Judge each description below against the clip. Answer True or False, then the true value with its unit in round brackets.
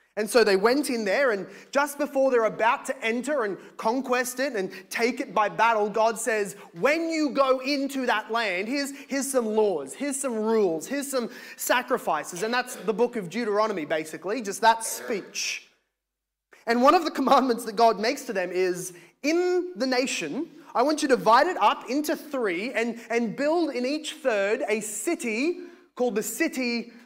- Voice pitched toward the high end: True (245 Hz)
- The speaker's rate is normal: True (185 wpm)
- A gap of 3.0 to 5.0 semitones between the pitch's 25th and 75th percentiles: True (4.2 semitones)